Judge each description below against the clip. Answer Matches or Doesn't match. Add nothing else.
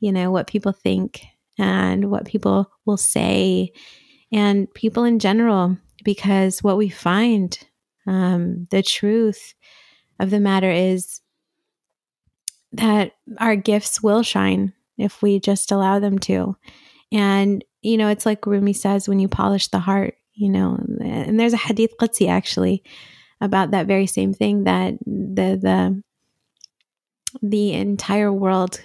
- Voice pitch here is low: Doesn't match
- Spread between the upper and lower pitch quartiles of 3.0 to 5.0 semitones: Doesn't match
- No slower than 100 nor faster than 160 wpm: Matches